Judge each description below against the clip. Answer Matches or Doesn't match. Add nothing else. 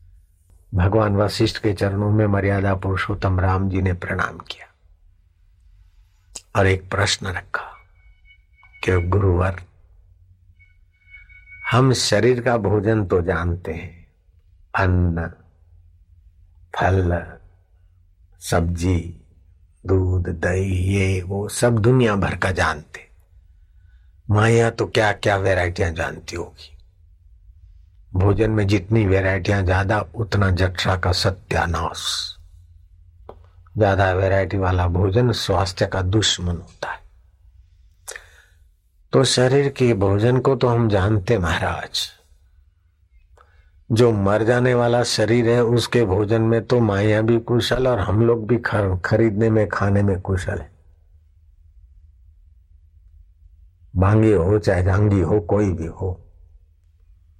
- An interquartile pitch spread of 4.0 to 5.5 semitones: Doesn't match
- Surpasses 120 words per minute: Doesn't match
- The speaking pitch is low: Matches